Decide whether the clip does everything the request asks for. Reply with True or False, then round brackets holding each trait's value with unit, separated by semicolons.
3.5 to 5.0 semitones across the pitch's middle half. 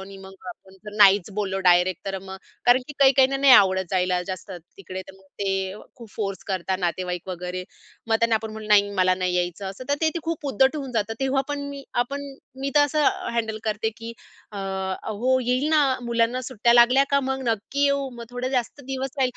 False (5.6 semitones)